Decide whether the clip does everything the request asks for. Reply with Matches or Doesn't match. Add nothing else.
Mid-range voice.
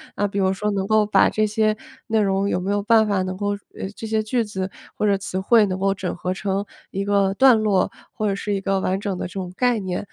Doesn't match